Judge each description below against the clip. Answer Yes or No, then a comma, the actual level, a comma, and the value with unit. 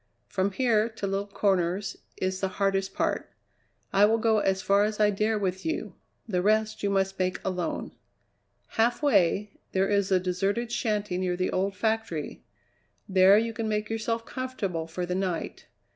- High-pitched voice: Yes, high, 200 Hz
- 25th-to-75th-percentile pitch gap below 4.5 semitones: Yes, narrow, 2.5 semitones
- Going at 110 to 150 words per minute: No, average, 165 wpm